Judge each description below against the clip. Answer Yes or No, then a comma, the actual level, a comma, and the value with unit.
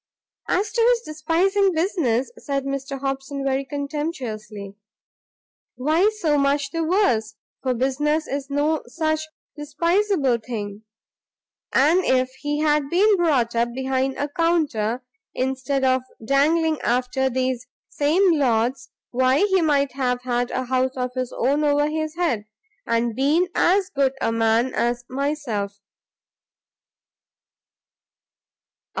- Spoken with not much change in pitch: No, average, 3.7 semitones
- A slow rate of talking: Yes, slow, 125 wpm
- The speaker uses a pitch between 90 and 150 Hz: No, very high, 275 Hz